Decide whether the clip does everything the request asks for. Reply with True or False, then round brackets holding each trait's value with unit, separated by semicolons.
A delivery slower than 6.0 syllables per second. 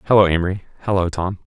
False (7.0 syllables/s)